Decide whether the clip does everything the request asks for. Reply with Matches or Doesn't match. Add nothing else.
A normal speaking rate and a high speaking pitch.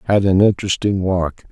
Doesn't match